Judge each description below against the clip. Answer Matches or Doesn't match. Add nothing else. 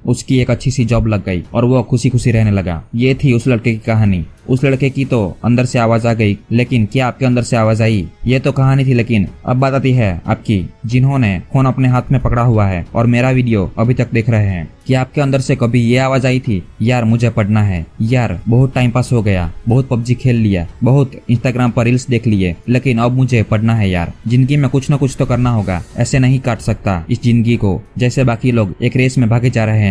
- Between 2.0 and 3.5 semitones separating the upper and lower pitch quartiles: Matches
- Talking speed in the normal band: Doesn't match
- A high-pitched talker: Doesn't match